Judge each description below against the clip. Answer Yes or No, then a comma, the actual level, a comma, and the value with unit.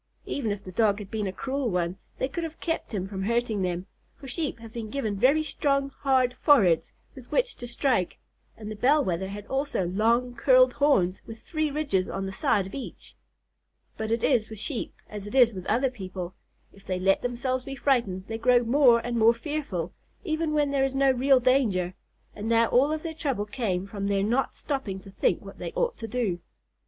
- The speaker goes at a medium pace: No, fast, 210 wpm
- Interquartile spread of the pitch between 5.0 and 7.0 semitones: Yes, wide, 5.5 semitones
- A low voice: No, high, 235 Hz